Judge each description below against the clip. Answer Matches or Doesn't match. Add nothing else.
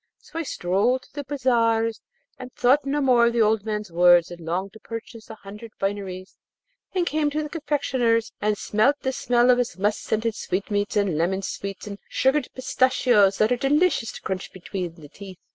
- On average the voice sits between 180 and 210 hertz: Doesn't match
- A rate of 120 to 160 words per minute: Doesn't match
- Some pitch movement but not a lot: Matches